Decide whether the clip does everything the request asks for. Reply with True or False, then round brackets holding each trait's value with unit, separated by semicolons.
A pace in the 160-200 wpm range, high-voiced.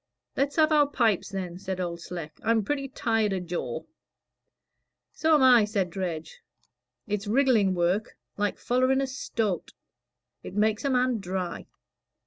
False (150 wpm; 210 Hz)